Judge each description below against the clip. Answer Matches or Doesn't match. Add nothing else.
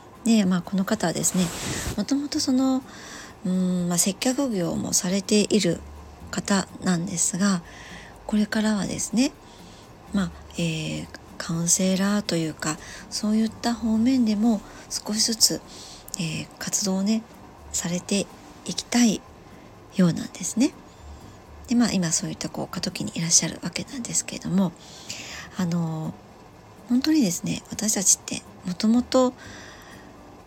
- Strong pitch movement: Doesn't match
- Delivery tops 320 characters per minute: Doesn't match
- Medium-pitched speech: Doesn't match